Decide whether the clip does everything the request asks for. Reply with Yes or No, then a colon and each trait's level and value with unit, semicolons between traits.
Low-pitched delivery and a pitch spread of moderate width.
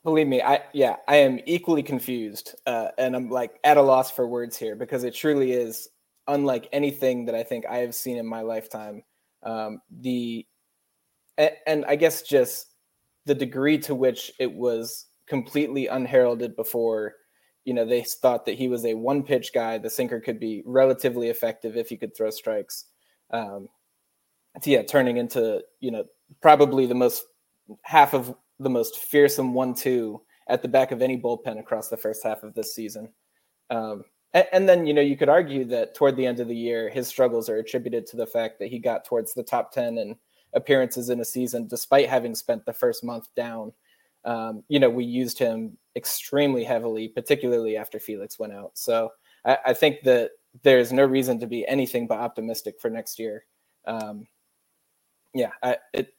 Yes: low, 125 Hz; average, 3.4 semitones